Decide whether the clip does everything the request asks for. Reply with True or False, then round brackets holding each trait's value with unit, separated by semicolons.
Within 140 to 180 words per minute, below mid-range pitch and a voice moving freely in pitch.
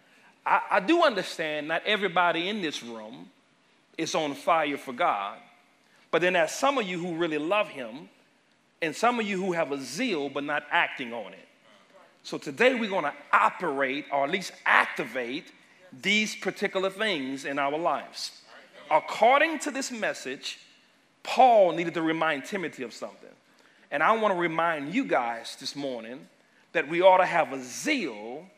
False (170 wpm; 175 Hz; 6.4 semitones)